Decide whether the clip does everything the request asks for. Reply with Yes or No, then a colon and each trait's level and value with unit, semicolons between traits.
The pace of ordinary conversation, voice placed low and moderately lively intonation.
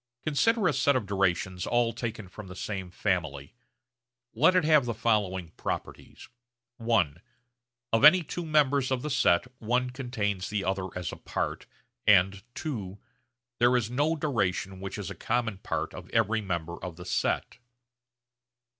No: average, 155 wpm; low, 110 Hz; wide, 5.7 semitones